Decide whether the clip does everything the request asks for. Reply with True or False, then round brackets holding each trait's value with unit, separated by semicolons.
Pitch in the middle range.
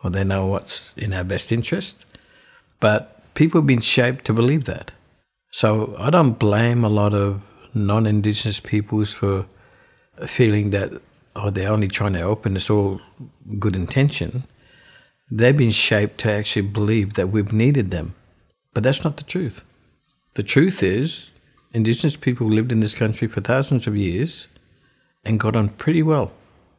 False (110 Hz)